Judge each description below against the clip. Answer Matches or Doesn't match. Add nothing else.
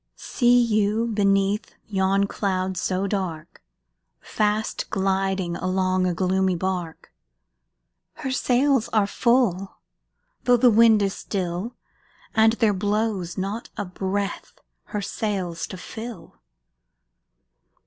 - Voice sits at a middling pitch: Doesn't match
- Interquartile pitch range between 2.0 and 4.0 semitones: Matches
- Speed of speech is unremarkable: Doesn't match